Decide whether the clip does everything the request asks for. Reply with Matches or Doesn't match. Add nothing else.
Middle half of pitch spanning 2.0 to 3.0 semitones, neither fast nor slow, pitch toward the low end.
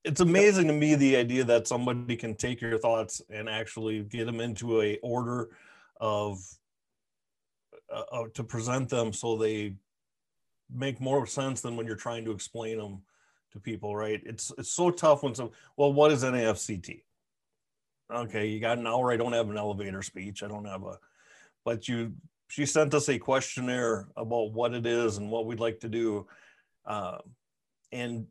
Matches